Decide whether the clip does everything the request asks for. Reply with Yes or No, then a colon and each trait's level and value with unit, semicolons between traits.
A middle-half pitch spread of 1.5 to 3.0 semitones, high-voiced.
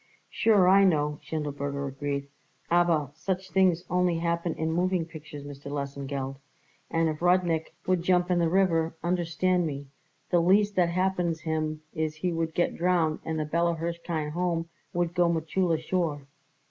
No: narrow, 2.5 semitones; medium, 165 Hz